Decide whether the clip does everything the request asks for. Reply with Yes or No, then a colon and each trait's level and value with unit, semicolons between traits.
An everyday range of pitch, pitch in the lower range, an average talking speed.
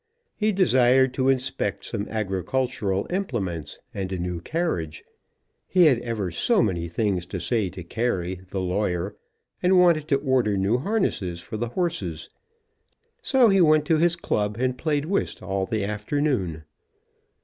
No: wide, 8.4 semitones; low, 115 Hz; average, 150 wpm